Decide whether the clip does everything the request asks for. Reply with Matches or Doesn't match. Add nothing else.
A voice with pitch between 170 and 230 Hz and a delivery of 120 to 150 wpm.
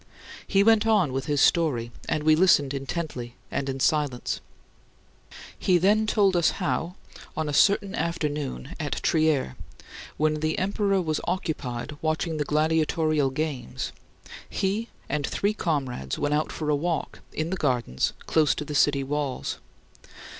Doesn't match